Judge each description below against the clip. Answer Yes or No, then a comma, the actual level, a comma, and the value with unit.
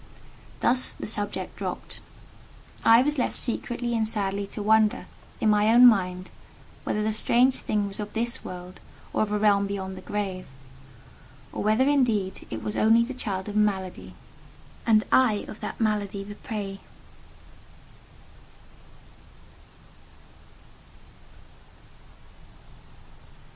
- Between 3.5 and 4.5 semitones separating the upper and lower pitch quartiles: No, narrow, 2.4 semitones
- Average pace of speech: No, slow, 120 wpm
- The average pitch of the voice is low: No, high, 210 Hz